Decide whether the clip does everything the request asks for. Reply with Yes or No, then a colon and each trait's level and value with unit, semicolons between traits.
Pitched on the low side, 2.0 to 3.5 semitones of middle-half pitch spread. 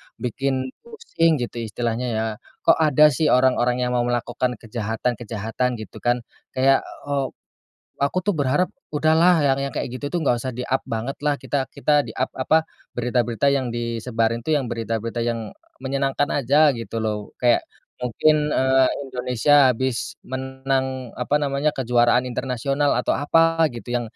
Yes: low, 130 Hz; average, 2.9 semitones